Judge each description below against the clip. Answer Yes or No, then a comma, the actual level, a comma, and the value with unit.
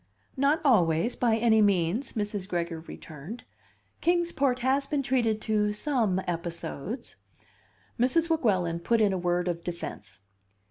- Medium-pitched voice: No, high, 210 Hz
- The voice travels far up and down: Yes, wide, 6.4 semitones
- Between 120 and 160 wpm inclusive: Yes, average, 140 wpm